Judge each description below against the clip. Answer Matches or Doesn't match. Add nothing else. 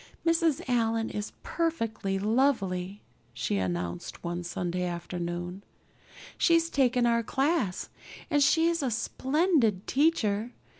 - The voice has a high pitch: Matches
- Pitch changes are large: Matches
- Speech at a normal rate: Doesn't match